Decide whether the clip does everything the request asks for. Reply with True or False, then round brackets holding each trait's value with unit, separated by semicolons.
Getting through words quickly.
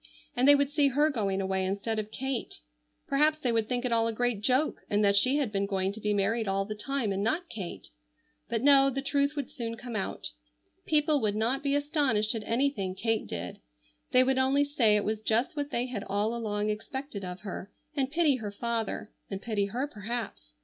True (215 wpm)